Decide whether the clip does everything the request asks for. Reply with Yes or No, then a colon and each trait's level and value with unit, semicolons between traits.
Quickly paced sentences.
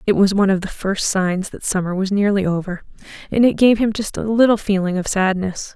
Yes: fast, 230 wpm